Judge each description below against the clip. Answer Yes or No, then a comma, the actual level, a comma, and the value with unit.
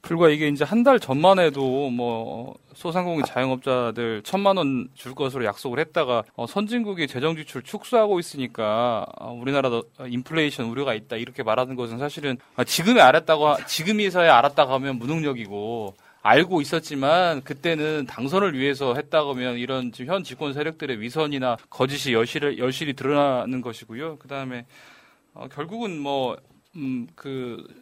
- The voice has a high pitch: No, medium, 140 Hz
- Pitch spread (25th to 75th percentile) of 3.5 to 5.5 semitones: Yes, average, 4.3 semitones